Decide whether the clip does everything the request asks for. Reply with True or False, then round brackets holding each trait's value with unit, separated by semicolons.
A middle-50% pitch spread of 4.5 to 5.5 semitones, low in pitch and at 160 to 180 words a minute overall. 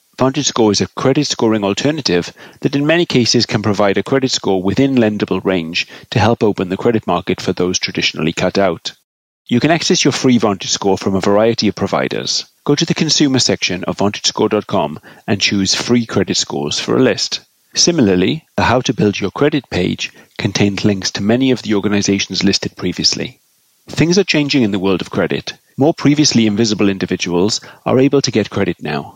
False (5.1 semitones; 105 Hz; 190 wpm)